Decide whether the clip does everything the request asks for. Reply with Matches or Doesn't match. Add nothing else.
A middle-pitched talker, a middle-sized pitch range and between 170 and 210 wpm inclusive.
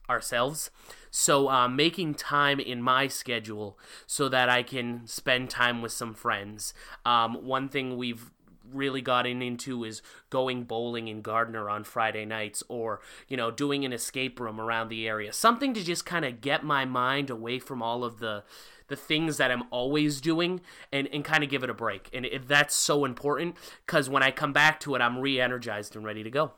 Doesn't match